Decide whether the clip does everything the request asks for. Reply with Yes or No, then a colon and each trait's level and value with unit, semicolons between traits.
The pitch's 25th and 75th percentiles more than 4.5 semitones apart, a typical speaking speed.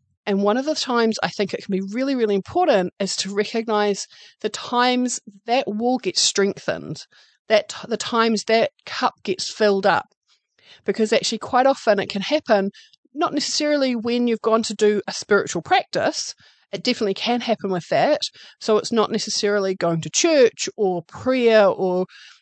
No: average, 3.9 semitones; average, 170 wpm